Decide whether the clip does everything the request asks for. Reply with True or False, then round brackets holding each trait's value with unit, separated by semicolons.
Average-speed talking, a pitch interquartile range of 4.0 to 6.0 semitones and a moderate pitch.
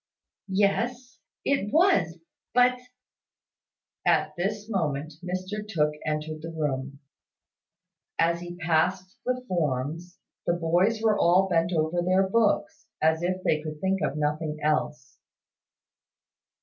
False (125 wpm; 4.5 semitones; 175 Hz)